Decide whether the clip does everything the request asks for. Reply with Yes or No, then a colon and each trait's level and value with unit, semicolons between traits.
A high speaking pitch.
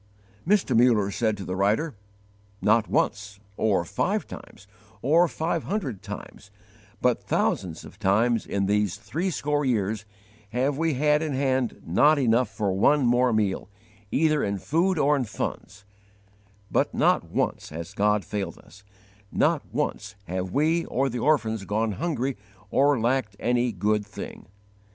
No: low, 115 Hz